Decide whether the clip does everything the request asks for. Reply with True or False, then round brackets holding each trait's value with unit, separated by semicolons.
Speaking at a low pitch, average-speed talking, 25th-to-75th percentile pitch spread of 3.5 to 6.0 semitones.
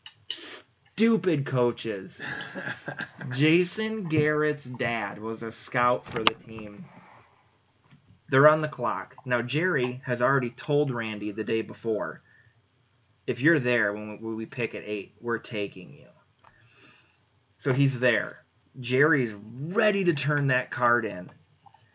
False (120 Hz; 125 wpm; 4.0 semitones)